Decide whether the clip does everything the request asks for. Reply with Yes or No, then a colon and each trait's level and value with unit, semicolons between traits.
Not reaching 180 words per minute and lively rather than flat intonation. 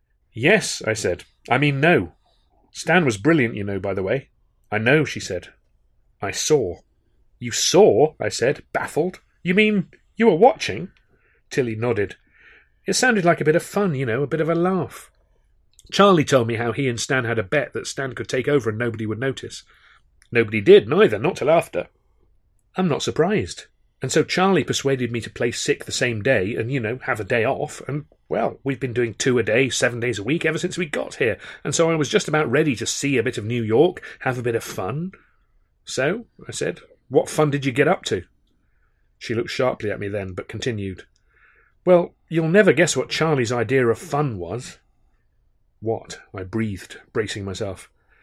No: average, 200 wpm; wide, 6.5 semitones